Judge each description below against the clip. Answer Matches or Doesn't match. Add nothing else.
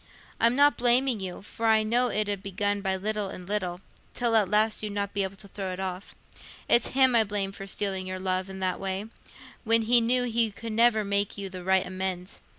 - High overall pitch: Matches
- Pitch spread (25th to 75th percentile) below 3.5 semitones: Matches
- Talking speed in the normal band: Doesn't match